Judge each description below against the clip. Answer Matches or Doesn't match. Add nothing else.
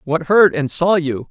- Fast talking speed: Matches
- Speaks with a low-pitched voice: Doesn't match